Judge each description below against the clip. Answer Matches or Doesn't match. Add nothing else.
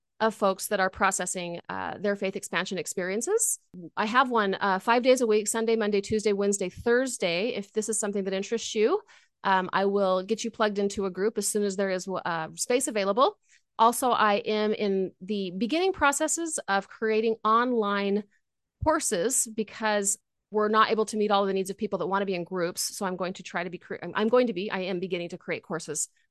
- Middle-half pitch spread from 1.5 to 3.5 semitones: Matches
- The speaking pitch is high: Matches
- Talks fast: Matches